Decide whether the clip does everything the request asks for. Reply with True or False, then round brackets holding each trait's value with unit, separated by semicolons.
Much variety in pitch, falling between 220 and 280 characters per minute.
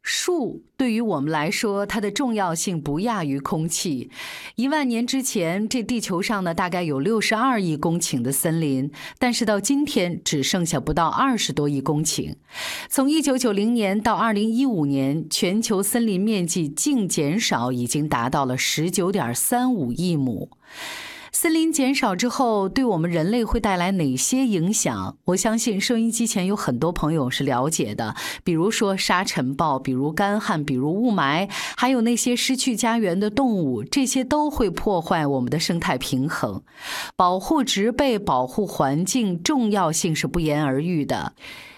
True (7.2 semitones; 255 characters per minute)